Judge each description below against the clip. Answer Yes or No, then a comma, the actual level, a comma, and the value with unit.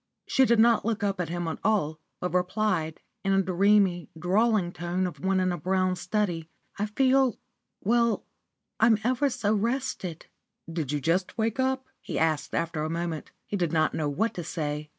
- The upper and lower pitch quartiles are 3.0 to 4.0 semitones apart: No, average, 4.7 semitones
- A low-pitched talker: No, medium, 185 Hz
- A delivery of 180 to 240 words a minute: Yes, average, 185 wpm